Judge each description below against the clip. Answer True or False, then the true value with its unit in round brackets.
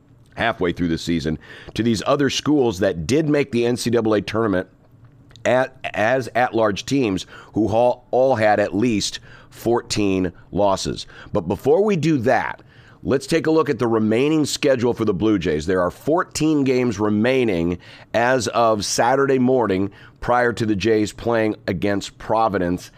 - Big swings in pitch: False (4.1 semitones)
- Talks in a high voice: False (120 Hz)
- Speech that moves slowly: False (155 wpm)